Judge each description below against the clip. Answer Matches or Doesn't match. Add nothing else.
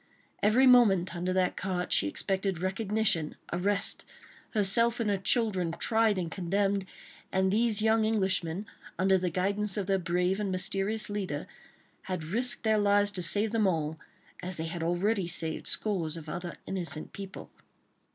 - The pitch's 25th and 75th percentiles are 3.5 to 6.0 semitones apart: Doesn't match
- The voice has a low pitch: Doesn't match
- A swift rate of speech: Doesn't match